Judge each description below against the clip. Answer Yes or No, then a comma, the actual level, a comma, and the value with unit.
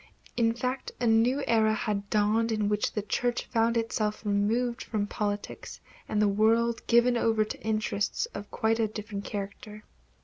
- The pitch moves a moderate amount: No, narrow, 1.8 semitones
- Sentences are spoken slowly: No, average, 165 wpm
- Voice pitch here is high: Yes, high, 220 Hz